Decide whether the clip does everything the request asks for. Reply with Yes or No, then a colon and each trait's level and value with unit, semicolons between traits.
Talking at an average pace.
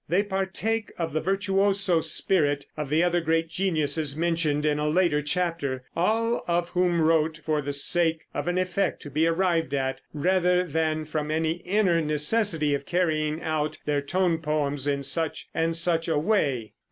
Yes: average, 170 wpm